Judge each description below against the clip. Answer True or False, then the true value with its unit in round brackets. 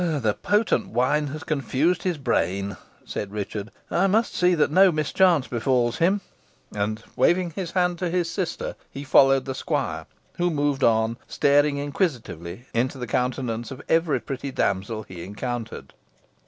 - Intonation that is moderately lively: False (6.7 semitones)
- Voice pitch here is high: False (140 Hz)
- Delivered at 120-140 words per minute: False (155 wpm)